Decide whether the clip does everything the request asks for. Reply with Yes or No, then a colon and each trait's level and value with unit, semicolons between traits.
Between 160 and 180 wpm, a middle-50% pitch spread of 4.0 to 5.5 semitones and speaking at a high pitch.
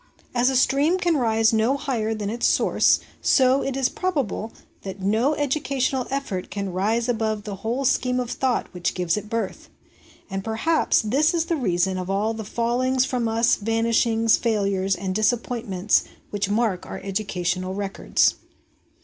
Yes: average, 165 wpm; average, 4.3 semitones; high, 225 Hz